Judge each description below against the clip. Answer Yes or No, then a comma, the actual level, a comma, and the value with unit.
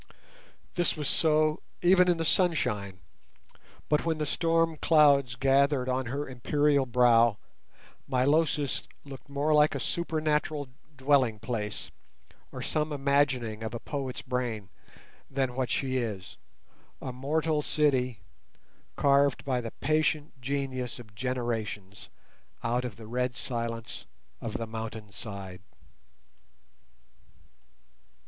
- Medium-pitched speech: No, low, 130 Hz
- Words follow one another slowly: Yes, slow, 115 wpm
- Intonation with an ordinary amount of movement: Yes, average, 4.3 semitones